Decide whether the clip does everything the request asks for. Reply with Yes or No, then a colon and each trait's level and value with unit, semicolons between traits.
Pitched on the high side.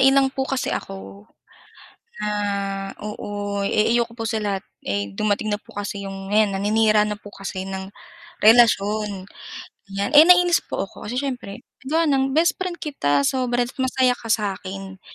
Yes: high, 210 Hz